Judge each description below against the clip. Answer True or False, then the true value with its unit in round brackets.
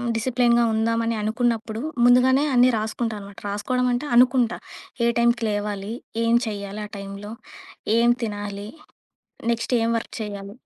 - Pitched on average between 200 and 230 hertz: True (225 Hz)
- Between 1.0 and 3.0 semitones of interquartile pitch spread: True (2.7 semitones)